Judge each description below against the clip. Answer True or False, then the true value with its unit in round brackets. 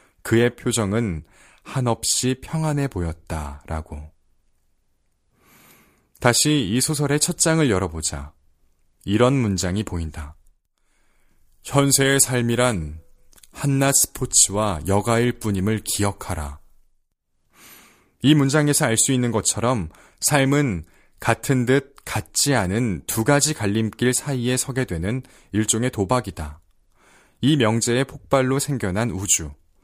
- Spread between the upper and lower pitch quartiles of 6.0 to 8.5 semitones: True (7.4 semitones)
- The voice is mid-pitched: False (110 Hz)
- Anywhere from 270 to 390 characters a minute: False (225 characters per minute)